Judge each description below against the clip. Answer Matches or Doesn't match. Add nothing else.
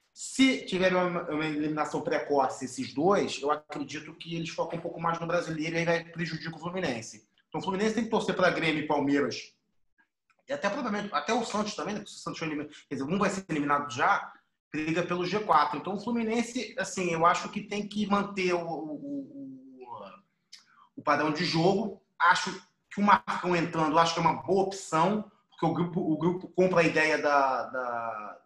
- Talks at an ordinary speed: Doesn't match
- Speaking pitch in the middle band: Matches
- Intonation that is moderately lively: Matches